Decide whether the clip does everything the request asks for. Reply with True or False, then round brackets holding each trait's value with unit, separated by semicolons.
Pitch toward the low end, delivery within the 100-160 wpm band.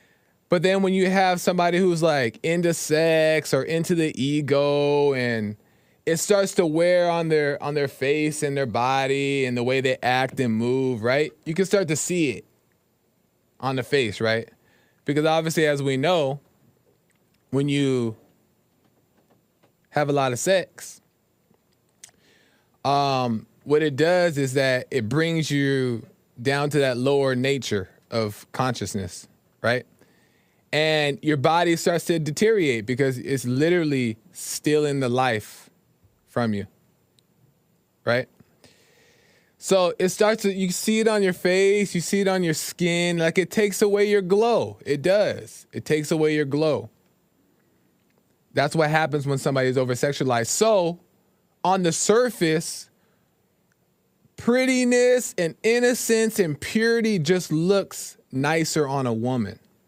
False (150 Hz; 140 wpm)